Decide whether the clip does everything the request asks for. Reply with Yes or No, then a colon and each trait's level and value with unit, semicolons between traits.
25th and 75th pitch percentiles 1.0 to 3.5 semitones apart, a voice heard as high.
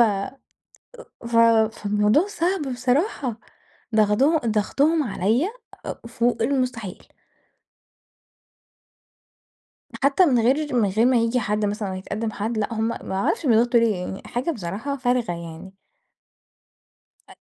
No: average, 4.1 semitones; high, 230 Hz